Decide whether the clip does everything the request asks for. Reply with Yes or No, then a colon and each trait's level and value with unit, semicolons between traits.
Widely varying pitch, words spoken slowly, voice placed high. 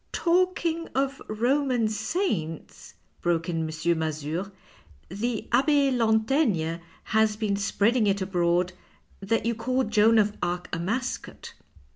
Yes: wide, 6.4 semitones; slow, 130 wpm; high, 215 Hz